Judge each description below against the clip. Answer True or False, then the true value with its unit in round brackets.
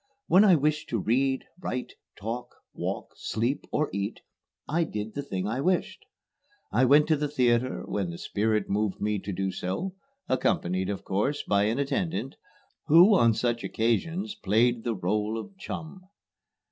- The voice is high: False (120 Hz)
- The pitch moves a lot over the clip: True (6.2 semitones)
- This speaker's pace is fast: False (160 wpm)